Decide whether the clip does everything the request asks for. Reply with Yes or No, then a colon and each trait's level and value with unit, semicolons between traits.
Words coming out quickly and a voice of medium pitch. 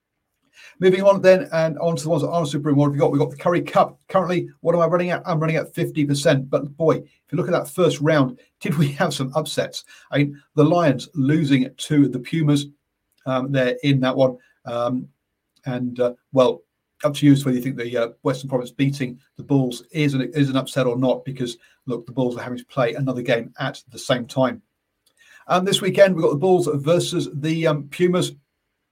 Yes: fast, 225 wpm; medium, 145 Hz